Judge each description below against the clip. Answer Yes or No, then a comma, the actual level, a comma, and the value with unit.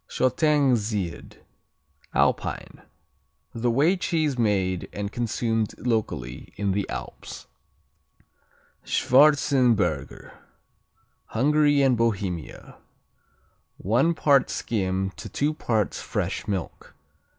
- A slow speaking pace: Yes, slow, 85 wpm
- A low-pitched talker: Yes, low, 115 Hz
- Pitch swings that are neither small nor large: No, wide, 5.7 semitones